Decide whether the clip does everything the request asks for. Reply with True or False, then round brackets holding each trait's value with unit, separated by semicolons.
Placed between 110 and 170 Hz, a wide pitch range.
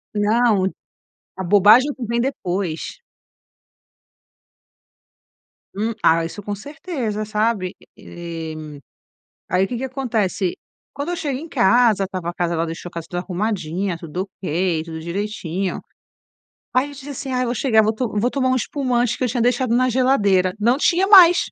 False (215 Hz; 5.7 semitones)